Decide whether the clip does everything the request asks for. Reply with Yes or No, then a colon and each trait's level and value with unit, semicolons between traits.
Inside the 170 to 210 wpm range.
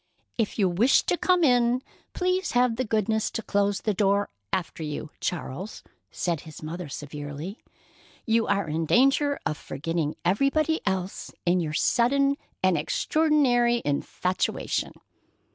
No: slow, 135 wpm